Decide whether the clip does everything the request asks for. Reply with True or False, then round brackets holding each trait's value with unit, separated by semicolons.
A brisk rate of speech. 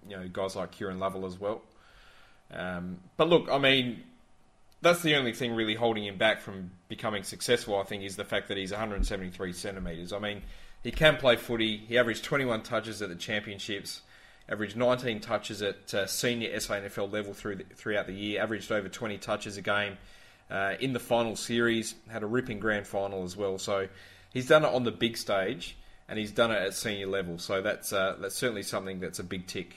True (215 wpm)